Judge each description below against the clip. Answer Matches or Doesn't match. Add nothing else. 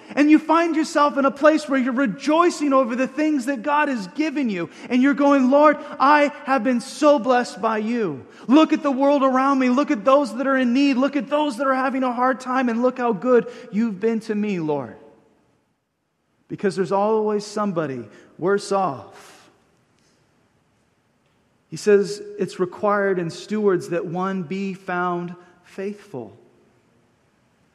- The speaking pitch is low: Doesn't match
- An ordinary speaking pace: Matches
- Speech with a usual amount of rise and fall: Doesn't match